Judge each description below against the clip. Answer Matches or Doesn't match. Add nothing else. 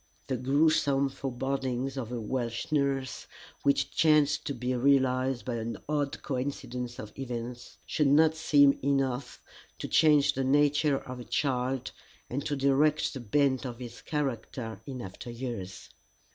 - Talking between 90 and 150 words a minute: Matches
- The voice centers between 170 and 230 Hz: Doesn't match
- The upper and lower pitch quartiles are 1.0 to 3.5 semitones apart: Matches